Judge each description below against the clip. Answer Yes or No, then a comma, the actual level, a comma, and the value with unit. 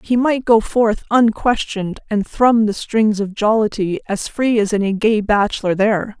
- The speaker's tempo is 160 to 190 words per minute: Yes, average, 175 wpm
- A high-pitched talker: Yes, high, 215 Hz